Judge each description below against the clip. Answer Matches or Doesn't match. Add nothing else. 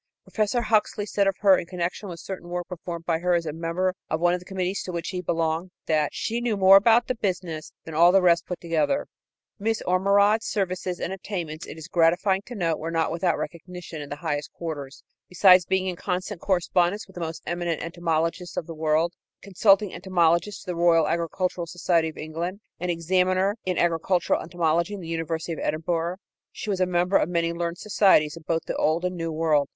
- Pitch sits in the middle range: Matches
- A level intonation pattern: Matches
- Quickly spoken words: Matches